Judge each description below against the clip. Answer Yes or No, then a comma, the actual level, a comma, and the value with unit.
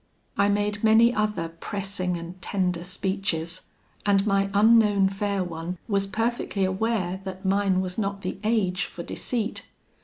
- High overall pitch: Yes, high, 195 Hz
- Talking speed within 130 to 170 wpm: Yes, average, 145 wpm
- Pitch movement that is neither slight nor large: No, narrow, 2.2 semitones